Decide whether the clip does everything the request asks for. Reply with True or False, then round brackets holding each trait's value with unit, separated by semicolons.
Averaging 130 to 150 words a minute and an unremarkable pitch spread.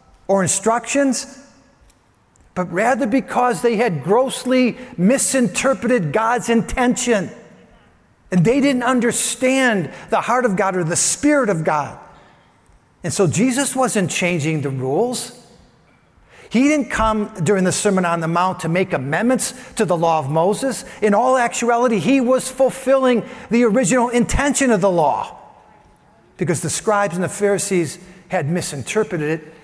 False (140 wpm; 5.7 semitones)